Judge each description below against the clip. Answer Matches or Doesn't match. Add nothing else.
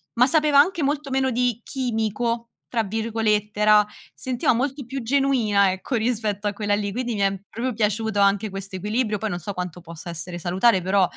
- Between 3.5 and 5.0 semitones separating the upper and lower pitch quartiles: Matches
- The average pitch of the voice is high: Matches